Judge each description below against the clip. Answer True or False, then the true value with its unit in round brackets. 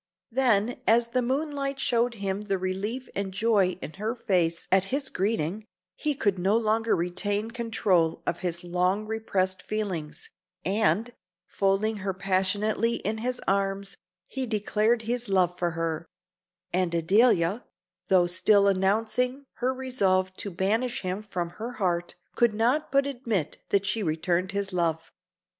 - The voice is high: True (200 Hz)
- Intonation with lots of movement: False (3.8 semitones)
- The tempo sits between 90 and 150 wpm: True (145 wpm)